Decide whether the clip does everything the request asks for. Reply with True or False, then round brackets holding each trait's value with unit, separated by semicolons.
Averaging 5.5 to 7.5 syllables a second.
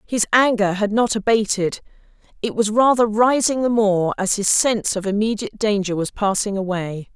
False (5.1 syllables/s)